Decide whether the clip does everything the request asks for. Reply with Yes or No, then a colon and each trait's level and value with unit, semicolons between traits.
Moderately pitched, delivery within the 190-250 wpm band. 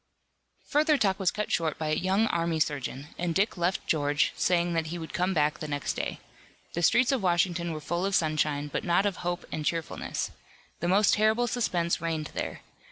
Yes: medium, 170 Hz; average, 200 wpm